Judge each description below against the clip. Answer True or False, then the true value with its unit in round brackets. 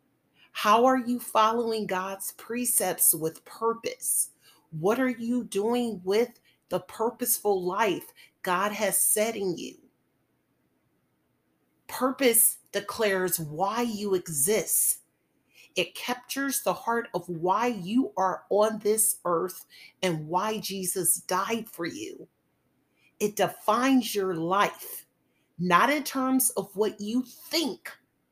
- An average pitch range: True (4.7 semitones)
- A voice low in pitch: False (215 Hz)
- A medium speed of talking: False (115 wpm)